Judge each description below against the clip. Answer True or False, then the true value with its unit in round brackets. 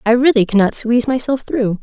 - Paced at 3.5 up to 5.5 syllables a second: False (5.8 syllables/s)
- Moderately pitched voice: False (235 Hz)